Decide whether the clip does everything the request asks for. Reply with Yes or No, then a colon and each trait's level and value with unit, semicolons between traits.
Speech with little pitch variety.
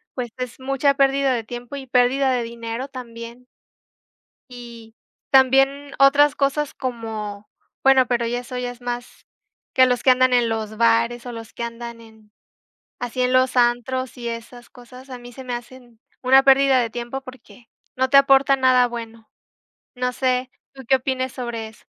Yes: narrow, 1.9 semitones